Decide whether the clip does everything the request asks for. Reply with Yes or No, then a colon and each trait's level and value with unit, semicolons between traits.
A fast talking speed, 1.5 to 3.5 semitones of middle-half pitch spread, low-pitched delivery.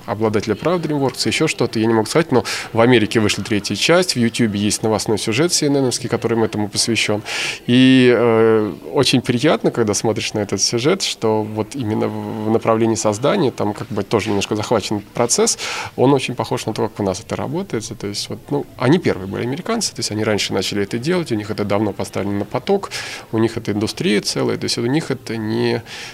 Yes: fast, 205 wpm; average, 3.0 semitones; low, 115 Hz